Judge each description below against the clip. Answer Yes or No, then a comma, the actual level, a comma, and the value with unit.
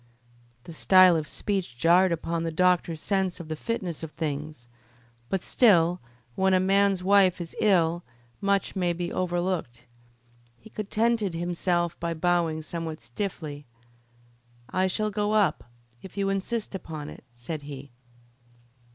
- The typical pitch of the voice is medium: Yes, medium, 175 Hz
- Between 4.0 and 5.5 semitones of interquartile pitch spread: No, average, 3.1 semitones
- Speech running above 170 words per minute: No, average, 140 wpm